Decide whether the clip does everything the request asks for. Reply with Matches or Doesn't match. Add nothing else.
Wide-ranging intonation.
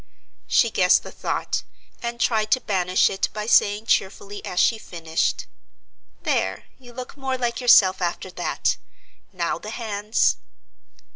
Doesn't match